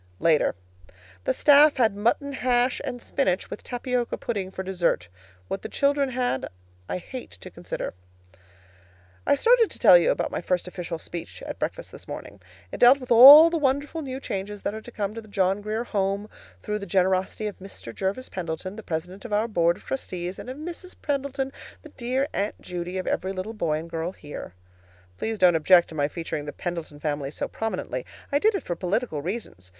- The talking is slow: No, average, 195 wpm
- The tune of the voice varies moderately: No, wide, 6.5 semitones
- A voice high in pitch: Yes, high, 205 Hz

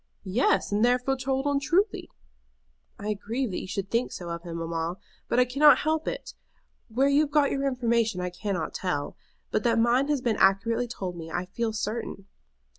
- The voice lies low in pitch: No, high, 230 Hz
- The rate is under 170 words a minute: No, average, 190 wpm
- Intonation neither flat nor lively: No, wide, 5.9 semitones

